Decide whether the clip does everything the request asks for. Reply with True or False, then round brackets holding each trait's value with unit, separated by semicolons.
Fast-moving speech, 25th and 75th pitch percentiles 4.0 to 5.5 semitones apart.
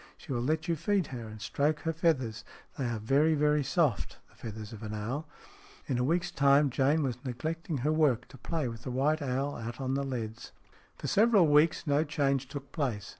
True (215 wpm; 4.3 semitones)